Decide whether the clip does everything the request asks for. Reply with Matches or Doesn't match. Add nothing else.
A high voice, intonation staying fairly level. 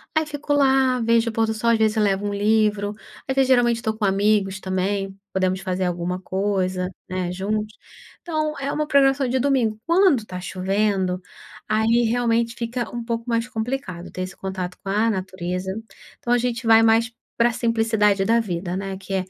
Doesn't match